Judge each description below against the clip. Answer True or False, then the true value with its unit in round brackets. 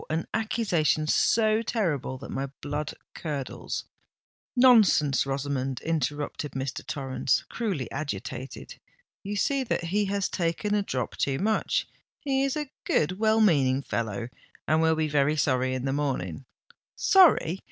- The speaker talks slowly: True (130 wpm)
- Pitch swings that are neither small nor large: False (7.4 semitones)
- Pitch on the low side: False (155 Hz)